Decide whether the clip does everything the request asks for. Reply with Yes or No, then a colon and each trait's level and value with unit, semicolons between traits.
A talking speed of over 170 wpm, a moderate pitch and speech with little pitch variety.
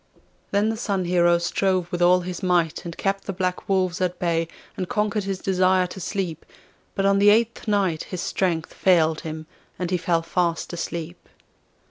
Yes: average, 180 wpm; medium, 180 Hz; narrow, 2.2 semitones